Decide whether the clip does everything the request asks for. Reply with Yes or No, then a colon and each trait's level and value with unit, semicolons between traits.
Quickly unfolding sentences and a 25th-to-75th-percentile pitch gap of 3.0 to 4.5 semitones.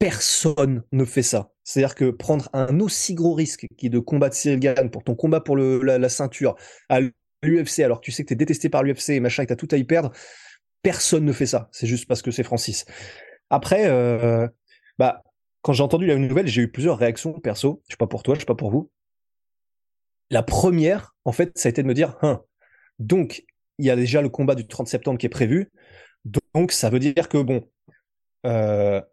Yes: fast, 225 wpm; average, 4.1 semitones